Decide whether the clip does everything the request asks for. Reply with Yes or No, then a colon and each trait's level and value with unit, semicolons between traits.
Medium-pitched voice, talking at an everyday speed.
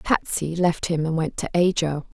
Yes: medium, 165 Hz; average, 190 wpm